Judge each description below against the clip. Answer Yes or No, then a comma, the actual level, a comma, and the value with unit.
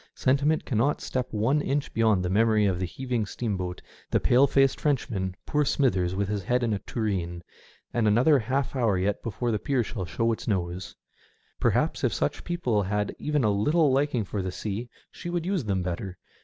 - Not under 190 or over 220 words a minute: Yes, average, 195 wpm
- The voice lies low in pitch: Yes, low, 110 Hz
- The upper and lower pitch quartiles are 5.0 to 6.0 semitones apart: Yes, wide, 5.6 semitones